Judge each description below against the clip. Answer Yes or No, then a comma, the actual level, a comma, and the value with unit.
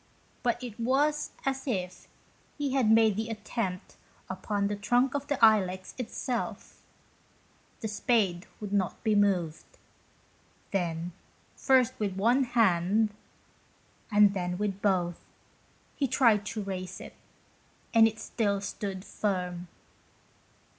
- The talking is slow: Yes, slow, 120 wpm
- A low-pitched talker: No, high, 210 Hz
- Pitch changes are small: No, average, 4.0 semitones